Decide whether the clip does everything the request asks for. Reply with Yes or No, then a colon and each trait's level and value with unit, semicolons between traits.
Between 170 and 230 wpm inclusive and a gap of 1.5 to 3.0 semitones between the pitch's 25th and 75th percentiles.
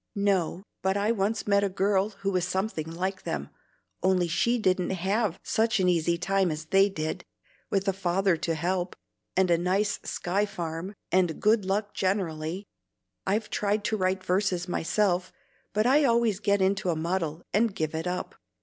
Yes: average, 175 wpm; narrow, 2.6 semitones